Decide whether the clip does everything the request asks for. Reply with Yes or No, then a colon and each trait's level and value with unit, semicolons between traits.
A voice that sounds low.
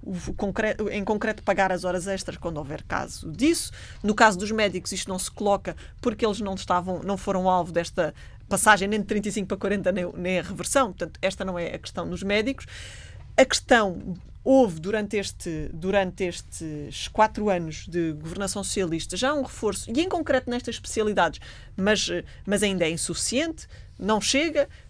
No: high, 200 Hz